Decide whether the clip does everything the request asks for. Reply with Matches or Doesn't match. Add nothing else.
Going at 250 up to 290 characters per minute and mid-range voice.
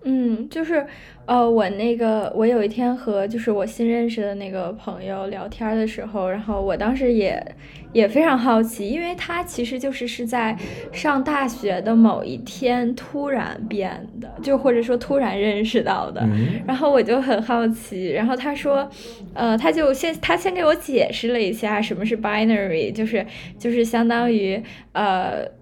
Doesn't match